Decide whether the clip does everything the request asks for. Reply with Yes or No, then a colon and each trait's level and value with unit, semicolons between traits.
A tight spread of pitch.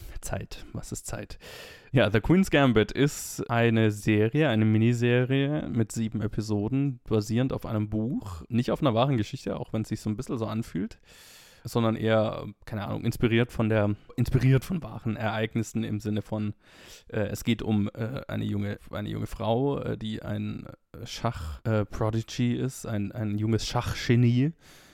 Yes: narrow, 2.3 semitones